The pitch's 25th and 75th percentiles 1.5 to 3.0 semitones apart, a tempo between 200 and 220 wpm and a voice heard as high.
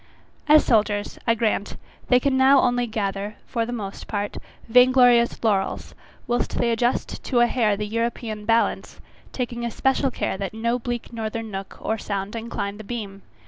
No: narrow, 2.6 semitones; average, 165 wpm; high, 230 Hz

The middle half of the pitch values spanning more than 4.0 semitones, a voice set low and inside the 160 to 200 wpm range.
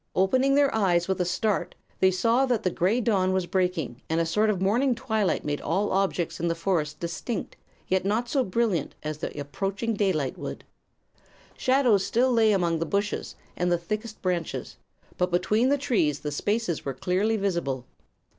No: average, 4.5 semitones; high, 190 Hz; average, 180 wpm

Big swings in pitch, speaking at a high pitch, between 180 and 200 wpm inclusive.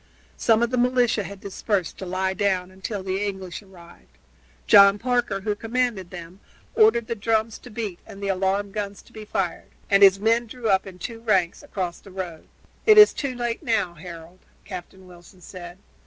No: average, 3.4 semitones; high, 200 Hz; average, 185 wpm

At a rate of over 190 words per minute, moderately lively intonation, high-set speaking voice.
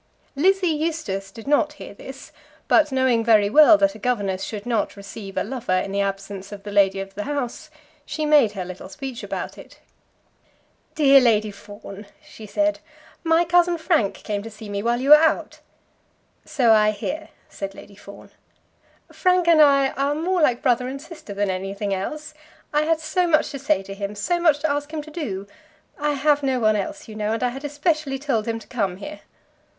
No: average, 200 wpm; wide, 6.9 semitones; very high, 255 Hz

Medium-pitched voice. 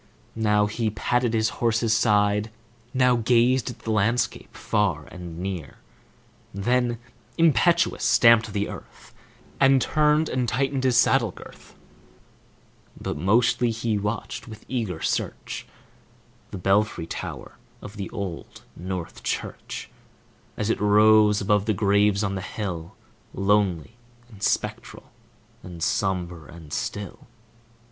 No: low, 105 Hz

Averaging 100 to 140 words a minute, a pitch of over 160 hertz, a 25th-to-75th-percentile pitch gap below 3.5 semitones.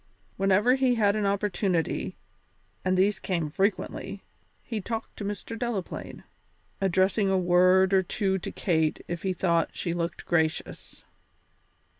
Yes: slow, 135 wpm; high, 190 Hz; average, 2.8 semitones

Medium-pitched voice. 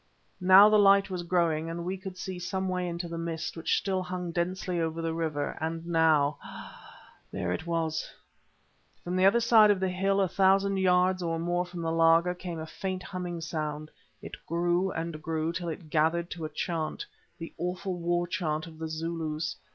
Yes: medium, 170 Hz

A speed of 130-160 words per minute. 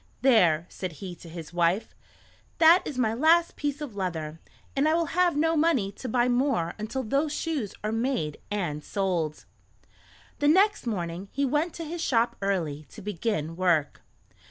No: average, 170 wpm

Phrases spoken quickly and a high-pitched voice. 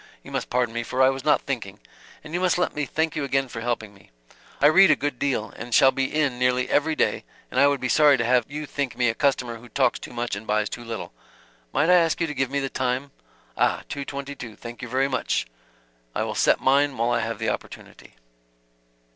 No: fast, 245 wpm; low, 130 Hz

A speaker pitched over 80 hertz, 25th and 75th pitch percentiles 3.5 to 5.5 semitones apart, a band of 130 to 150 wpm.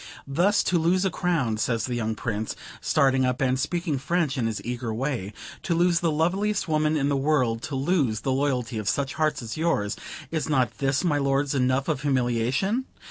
No: low, 135 Hz; average, 4.6 semitones; average, 195 wpm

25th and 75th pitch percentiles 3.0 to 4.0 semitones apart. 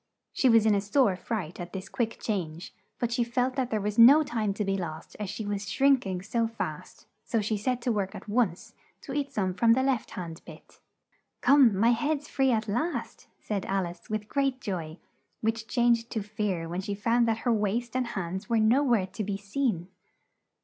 Yes: average, 3.7 semitones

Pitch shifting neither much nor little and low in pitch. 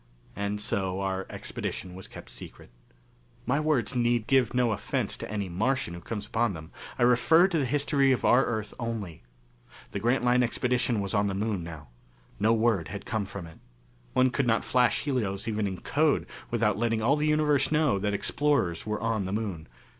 Yes: average, 4.3 semitones; low, 115 Hz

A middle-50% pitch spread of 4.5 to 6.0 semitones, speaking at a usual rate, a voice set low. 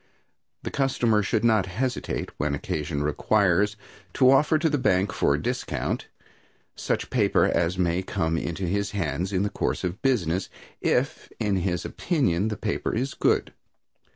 Yes: average, 5.0 semitones; average, 155 wpm; very low, 95 Hz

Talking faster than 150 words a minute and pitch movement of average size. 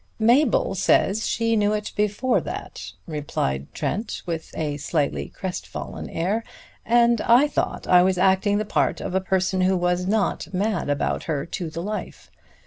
Yes: average, 160 wpm; average, 3.8 semitones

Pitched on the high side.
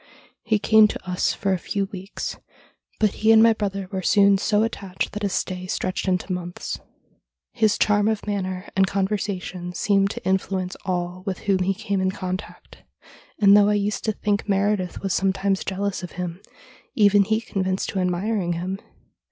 Yes: high, 195 Hz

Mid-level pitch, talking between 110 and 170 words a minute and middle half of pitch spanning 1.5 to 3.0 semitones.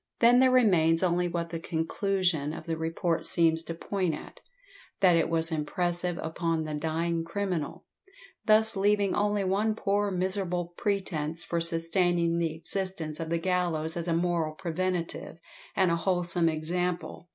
Yes: medium, 170 Hz; average, 150 wpm; narrow, 2.4 semitones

